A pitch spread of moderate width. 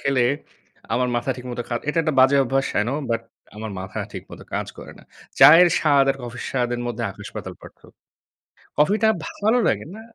Yes: average, 3.7 semitones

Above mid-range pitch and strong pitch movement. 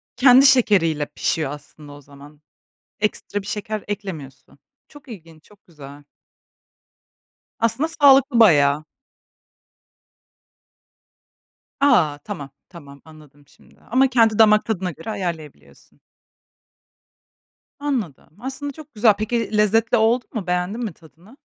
Yes: high, 205 Hz; wide, 7.0 semitones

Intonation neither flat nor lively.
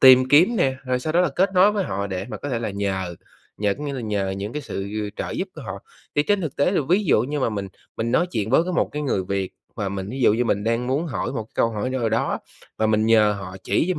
No: wide, 6.4 semitones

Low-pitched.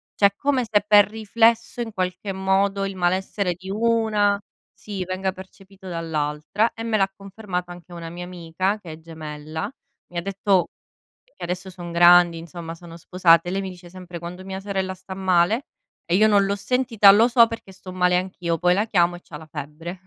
No: medium, 185 Hz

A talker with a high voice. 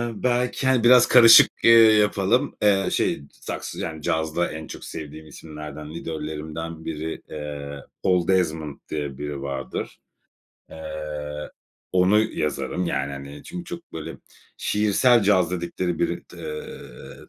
No: very low, 80 Hz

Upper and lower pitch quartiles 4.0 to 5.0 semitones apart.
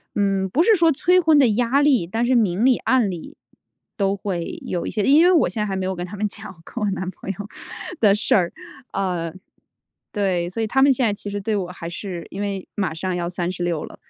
Yes: average, 4.6 semitones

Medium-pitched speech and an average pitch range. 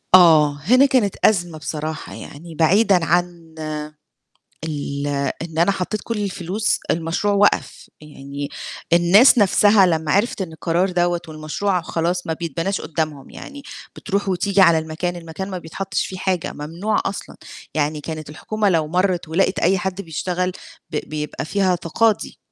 Yes: medium, 175 Hz; average, 3.5 semitones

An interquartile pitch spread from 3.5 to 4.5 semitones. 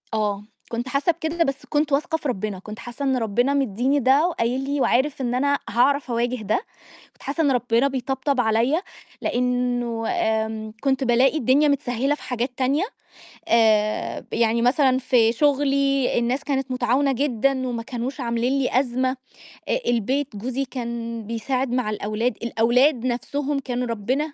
No: average, 2.9 semitones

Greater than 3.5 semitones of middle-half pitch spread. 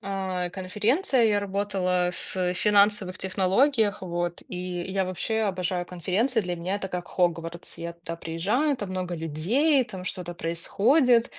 No: average, 3.0 semitones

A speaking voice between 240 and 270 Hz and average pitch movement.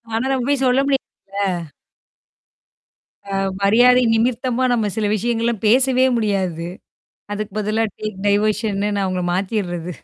No: high, 215 Hz; average, 3.5 semitones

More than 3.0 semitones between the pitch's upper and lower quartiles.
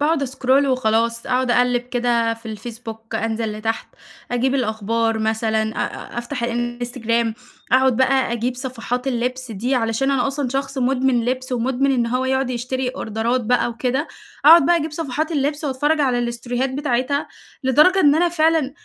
No: narrow, 2.5 semitones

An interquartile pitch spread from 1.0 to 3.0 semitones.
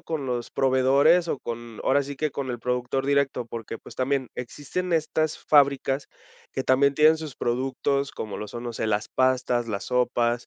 Yes: average, 2.7 semitones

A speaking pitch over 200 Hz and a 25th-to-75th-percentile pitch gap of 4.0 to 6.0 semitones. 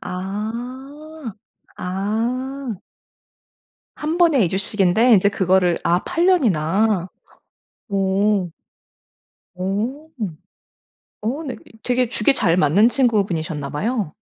Yes: high, 210 Hz; wide, 5.5 semitones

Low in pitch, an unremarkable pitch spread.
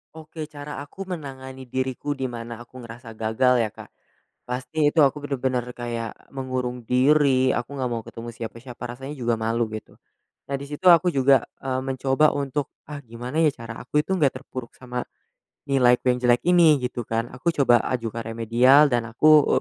Yes: low, 130 Hz; average, 3.2 semitones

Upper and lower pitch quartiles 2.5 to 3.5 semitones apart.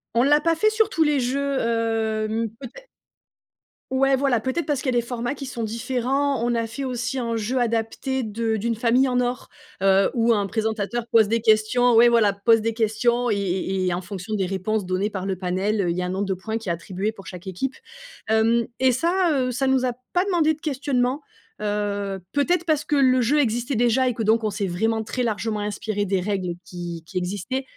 No: average, 4.1 semitones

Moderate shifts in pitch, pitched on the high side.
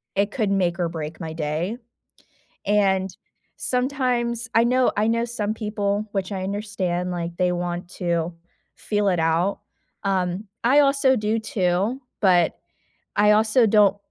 Yes: average, 3.9 semitones; high, 200 Hz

